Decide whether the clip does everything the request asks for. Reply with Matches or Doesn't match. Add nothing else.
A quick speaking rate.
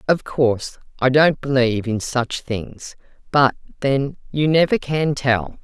Doesn't match